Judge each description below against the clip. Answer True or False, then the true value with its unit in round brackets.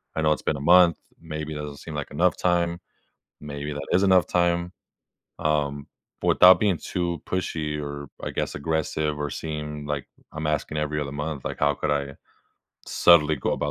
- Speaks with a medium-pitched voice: False (75 Hz)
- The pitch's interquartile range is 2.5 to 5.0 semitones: True (2.8 semitones)